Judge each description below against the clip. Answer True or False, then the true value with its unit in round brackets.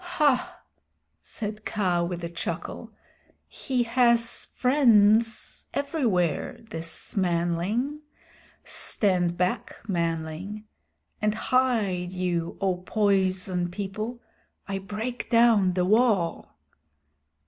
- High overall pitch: True (200 Hz)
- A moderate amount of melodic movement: True (4.7 semitones)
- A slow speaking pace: True (90 wpm)